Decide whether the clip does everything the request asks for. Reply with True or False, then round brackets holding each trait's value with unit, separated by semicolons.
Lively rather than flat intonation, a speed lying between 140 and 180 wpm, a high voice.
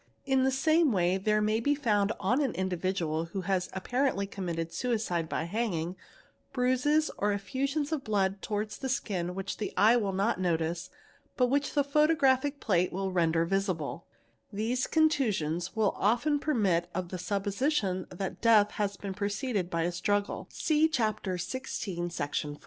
True (6.0 semitones; 160 wpm; 205 Hz)